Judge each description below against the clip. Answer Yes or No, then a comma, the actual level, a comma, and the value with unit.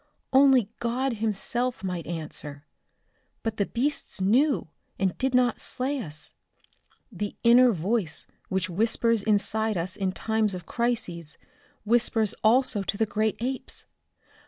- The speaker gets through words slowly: Yes, slow, 130 wpm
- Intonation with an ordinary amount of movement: Yes, average, 4.2 semitones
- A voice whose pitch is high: Yes, high, 220 Hz